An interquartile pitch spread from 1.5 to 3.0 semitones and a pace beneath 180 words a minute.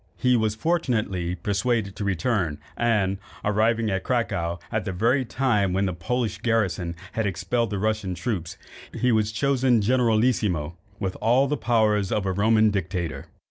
No: average, 3.7 semitones; average, 155 wpm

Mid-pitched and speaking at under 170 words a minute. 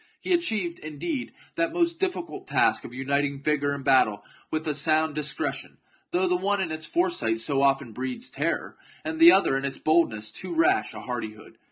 No: medium, 155 Hz; average, 185 wpm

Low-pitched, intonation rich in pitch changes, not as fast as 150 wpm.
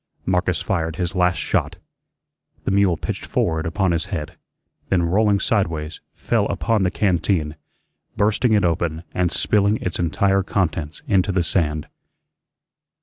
No: very low, 90 Hz; average, 3.3 semitones; average, 140 wpm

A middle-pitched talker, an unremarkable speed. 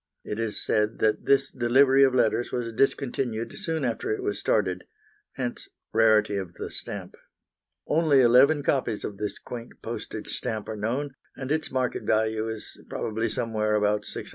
No: low, 115 Hz; average, 165 wpm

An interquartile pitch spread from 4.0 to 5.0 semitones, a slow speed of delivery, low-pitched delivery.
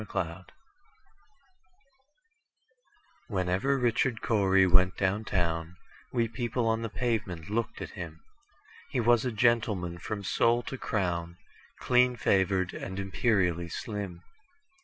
Yes: average, 4.5 semitones; slow, 105 wpm; low, 100 Hz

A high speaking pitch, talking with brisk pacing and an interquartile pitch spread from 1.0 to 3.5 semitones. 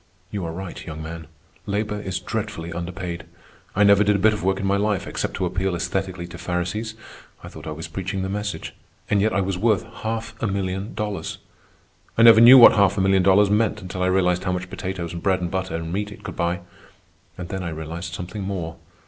No: very low, 95 Hz; fast, 215 wpm; average, 2.8 semitones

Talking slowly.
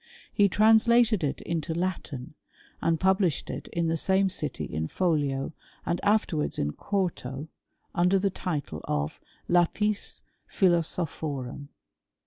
Yes: slow, 120 wpm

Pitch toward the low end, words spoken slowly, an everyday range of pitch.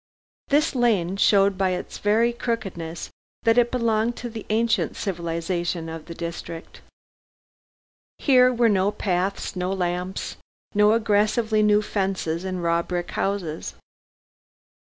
No: high, 195 Hz; slow, 125 wpm; average, 4.3 semitones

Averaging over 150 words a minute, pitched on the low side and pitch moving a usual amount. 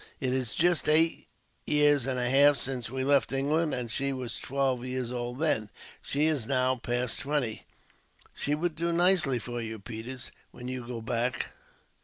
Yes: average, 175 wpm; low, 130 Hz; average, 3.2 semitones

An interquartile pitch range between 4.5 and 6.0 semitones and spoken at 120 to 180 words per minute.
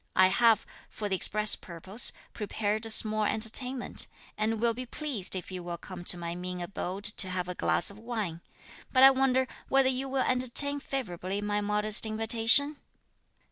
Yes: average, 5.1 semitones; average, 175 wpm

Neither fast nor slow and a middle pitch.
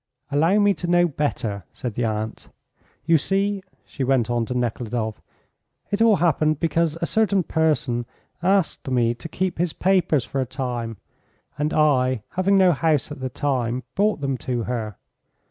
Yes: average, 165 wpm; medium, 145 Hz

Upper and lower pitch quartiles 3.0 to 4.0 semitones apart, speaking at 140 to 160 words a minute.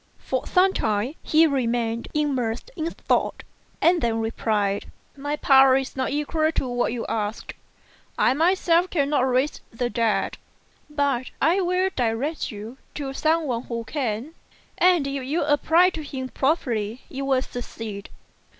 No: average, 4.8 semitones; average, 150 wpm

